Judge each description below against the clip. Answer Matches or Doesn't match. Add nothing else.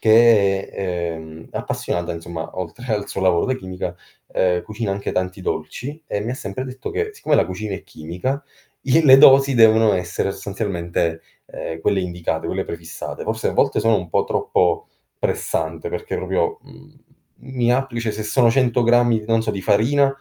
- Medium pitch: Doesn't match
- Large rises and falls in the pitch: Matches